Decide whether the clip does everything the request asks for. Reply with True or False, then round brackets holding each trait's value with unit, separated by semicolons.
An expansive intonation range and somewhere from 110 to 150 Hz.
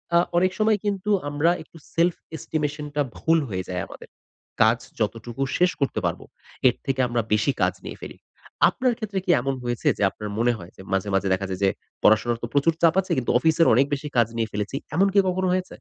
True (7.6 semitones; 135 Hz)